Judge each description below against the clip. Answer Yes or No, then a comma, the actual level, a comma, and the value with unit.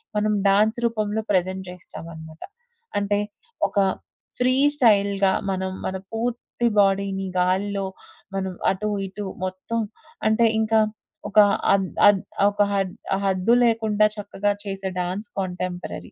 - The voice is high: Yes, high, 200 Hz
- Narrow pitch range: Yes, narrow, 2.2 semitones